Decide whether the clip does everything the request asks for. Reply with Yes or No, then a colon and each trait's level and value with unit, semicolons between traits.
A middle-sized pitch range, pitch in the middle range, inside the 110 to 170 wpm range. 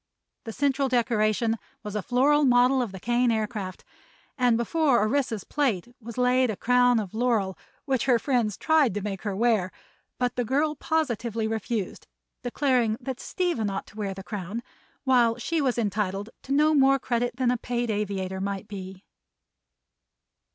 No: average, 3.5 semitones; high, 235 Hz; average, 165 wpm